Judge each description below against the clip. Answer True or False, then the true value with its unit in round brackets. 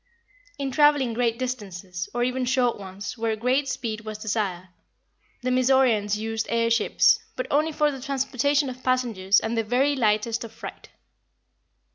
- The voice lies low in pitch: False (235 Hz)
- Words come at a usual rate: True (155 wpm)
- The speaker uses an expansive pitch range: False (3.3 semitones)